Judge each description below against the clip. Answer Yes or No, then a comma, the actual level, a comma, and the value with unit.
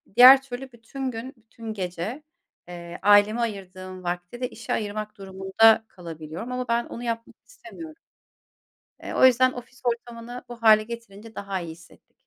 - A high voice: Yes, high, 225 Hz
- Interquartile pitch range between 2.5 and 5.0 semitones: Yes, average, 4.2 semitones